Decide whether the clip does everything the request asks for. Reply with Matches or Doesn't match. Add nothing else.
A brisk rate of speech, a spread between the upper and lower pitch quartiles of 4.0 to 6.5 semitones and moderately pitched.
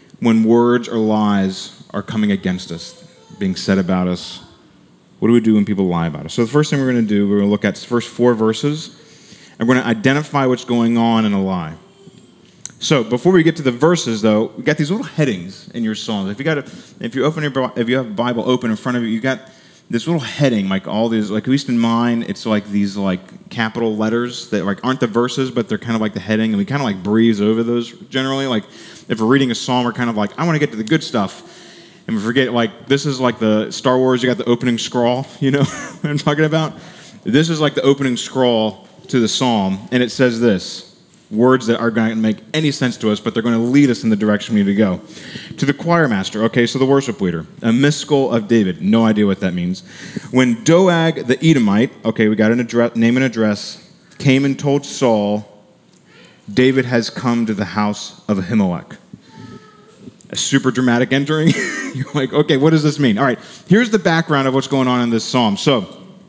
Doesn't match